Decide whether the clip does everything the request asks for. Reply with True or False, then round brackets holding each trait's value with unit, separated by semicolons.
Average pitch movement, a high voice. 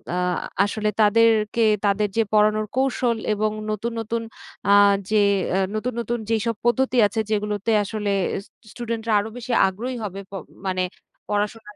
False (1.9 semitones; 215 Hz)